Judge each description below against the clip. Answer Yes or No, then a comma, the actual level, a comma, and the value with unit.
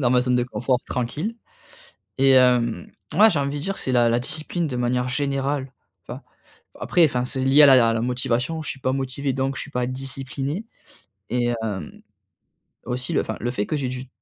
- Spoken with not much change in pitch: Yes, narrow, 2.1 semitones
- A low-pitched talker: Yes, low, 130 Hz